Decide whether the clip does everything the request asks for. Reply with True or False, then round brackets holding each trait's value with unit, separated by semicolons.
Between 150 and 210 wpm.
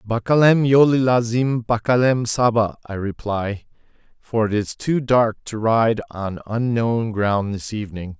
False (140 wpm)